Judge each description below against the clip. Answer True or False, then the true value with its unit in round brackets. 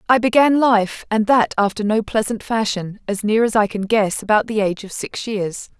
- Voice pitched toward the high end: True (215 Hz)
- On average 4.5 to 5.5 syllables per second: True (5.0 syllables/s)